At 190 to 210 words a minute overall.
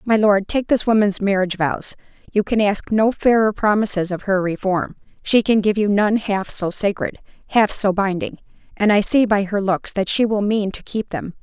Yes: average, 200 wpm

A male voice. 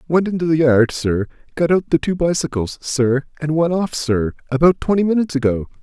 Yes: male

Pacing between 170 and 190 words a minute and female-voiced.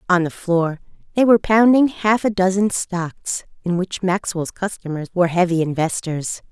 No: average, 155 wpm; female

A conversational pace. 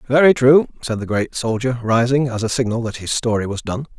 No: fast, 225 wpm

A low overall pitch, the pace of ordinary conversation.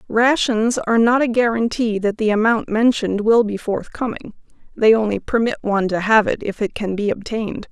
No: high, 220 Hz; average, 185 wpm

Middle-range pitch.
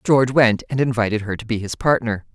No: low, 115 Hz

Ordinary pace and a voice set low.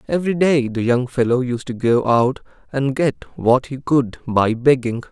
Yes: average, 190 wpm; low, 130 Hz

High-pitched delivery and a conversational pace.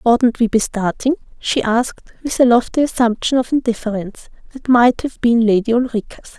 Yes: high, 235 Hz; average, 170 wpm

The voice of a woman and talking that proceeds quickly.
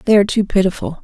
Yes: female; fast, 230 wpm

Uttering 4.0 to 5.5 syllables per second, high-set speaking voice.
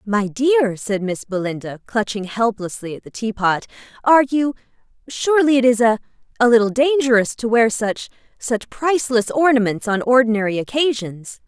Yes: 5.1 syllables/s; high, 230 Hz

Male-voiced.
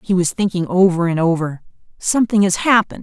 No: female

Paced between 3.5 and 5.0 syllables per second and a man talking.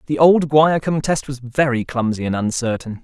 Yes: 4.9 syllables/s; male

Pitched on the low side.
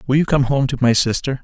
Yes: low, 130 Hz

